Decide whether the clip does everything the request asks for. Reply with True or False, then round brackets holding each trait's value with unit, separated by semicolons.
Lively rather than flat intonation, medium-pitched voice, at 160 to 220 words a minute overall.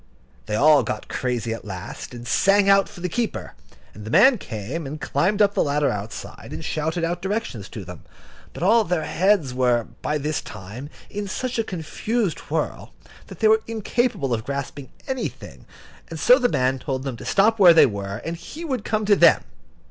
True (8.6 semitones; 160 Hz; 195 wpm)